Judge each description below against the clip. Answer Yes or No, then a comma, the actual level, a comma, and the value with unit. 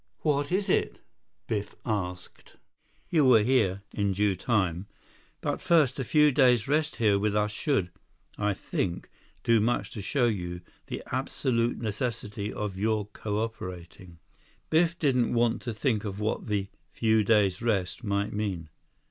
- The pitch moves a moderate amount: Yes, average, 3.7 semitones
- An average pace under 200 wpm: Yes, average, 150 wpm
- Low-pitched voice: Yes, low, 105 Hz